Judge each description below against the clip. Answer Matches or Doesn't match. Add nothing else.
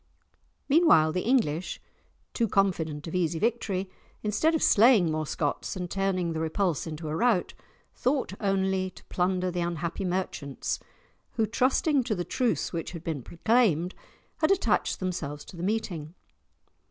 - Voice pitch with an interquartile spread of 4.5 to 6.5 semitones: Matches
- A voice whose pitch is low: Doesn't match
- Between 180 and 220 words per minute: Doesn't match